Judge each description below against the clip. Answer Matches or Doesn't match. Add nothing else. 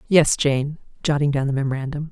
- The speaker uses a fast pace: Doesn't match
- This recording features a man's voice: Doesn't match